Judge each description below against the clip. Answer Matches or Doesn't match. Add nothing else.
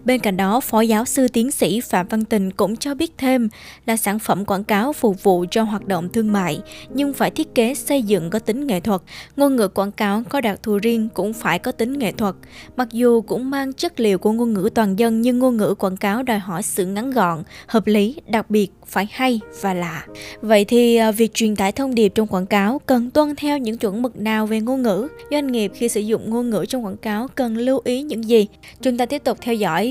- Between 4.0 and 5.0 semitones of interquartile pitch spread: Doesn't match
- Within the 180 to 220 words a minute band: Doesn't match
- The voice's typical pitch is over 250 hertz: Doesn't match